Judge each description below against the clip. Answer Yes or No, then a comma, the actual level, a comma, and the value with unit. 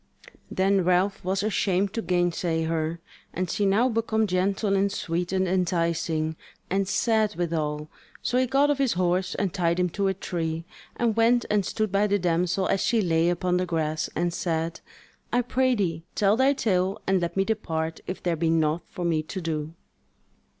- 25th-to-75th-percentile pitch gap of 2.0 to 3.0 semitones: No, average, 3.4 semitones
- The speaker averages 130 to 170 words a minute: No, average, 185 wpm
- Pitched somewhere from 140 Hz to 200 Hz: Yes, medium, 185 Hz